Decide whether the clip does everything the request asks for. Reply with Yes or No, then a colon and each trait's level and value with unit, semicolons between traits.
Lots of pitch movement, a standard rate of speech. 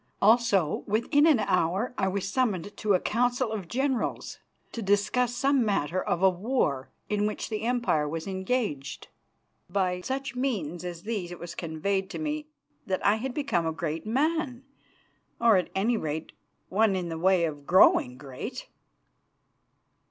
Yes: wide, 5.8 semitones; average, 160 wpm